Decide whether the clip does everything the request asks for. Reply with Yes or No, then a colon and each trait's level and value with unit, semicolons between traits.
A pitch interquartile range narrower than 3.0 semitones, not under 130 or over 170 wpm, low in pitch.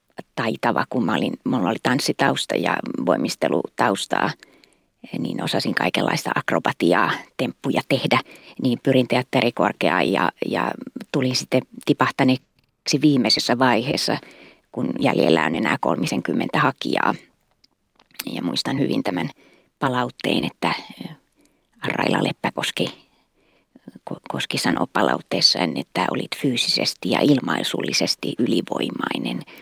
No: narrow, 2.4 semitones; slow, 95 wpm; low, 130 Hz